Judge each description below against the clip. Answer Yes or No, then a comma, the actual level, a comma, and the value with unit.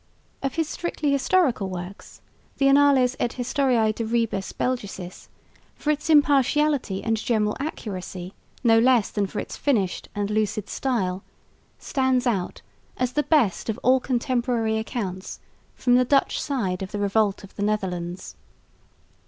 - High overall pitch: Yes, high, 230 Hz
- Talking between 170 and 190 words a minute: No, average, 145 wpm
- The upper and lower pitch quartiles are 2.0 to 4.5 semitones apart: No, average, 5.0 semitones